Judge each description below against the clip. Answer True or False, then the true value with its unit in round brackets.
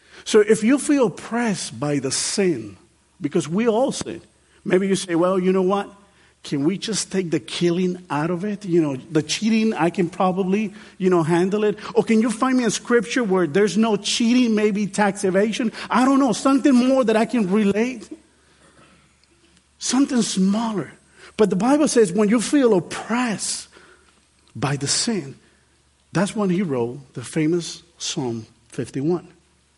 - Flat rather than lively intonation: False (4.7 semitones)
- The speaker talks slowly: False (165 wpm)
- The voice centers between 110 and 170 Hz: False (200 Hz)